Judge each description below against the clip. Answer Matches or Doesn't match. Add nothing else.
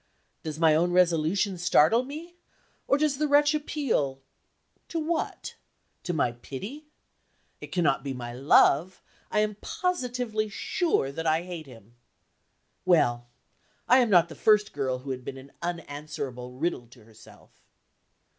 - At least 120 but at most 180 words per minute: Matches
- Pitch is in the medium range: Matches